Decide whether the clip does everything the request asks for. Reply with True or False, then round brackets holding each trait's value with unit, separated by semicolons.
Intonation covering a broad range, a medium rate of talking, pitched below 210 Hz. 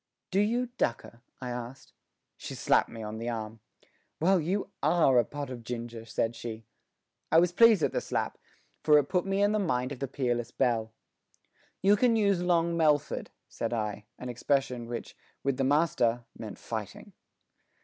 True (6.9 semitones; 170 wpm; 135 Hz)